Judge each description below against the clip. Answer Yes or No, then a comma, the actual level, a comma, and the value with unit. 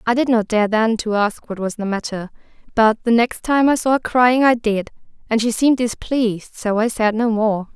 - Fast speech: Yes, fast, 225 wpm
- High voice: Yes, high, 225 Hz